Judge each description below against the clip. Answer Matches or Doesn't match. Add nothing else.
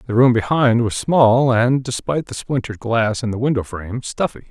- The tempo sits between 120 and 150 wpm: Doesn't match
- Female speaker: Doesn't match